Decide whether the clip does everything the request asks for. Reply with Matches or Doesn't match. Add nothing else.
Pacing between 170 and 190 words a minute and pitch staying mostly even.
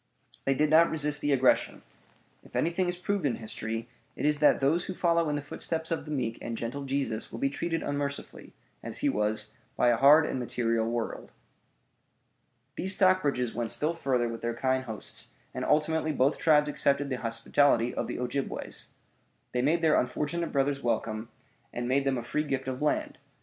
Doesn't match